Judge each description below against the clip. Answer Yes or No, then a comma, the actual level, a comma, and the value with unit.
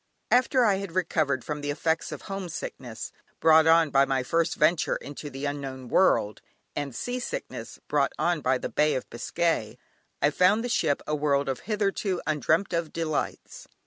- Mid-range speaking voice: Yes, medium, 155 Hz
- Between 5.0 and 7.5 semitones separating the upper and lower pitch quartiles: No, average, 4.5 semitones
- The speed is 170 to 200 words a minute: Yes, average, 175 wpm